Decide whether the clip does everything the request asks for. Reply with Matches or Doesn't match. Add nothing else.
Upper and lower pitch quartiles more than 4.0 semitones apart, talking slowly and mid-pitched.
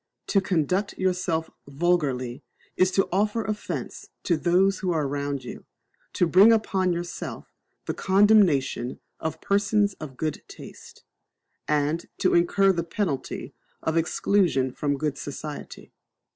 Matches